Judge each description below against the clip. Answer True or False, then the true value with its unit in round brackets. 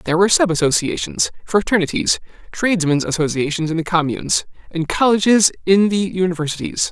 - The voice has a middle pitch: True (175 Hz)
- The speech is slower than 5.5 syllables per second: False (6.0 syllables/s)